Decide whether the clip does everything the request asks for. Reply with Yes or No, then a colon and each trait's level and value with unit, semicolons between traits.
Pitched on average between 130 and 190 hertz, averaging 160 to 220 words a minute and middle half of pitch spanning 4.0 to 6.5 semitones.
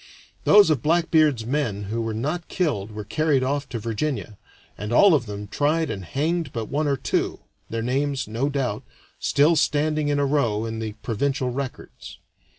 Yes: low, 135 Hz; average, 175 wpm; average, 5.2 semitones